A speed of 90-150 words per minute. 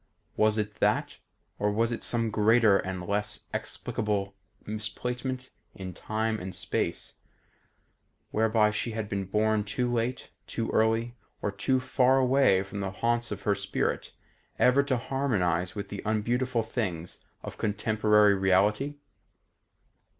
Yes: slow, 135 wpm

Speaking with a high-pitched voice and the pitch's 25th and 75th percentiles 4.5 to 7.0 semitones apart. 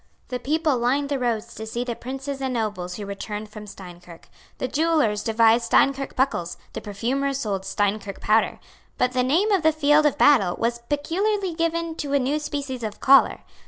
Yes: very high, 255 Hz; average, 5.2 semitones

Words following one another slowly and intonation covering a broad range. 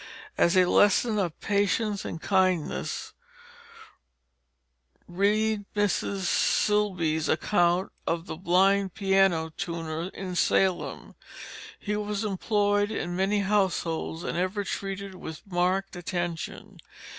No: slow, 105 wpm; average, 2.8 semitones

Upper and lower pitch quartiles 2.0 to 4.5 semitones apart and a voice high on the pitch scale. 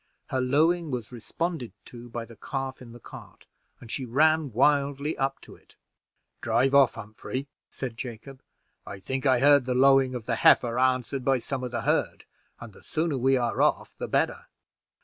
No: narrow, 2.6 semitones; low, 130 Hz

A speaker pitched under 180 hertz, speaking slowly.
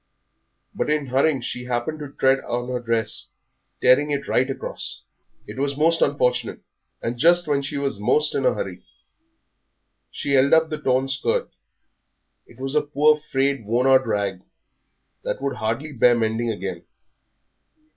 No: low, 135 Hz; average, 155 wpm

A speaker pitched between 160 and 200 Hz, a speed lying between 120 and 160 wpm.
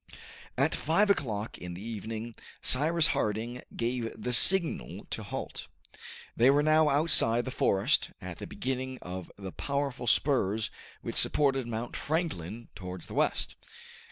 No: low, 120 Hz; average, 140 wpm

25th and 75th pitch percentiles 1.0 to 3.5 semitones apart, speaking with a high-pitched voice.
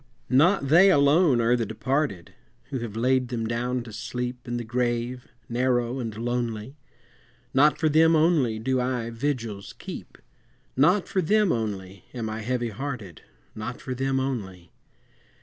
No: average, 3.1 semitones; low, 125 Hz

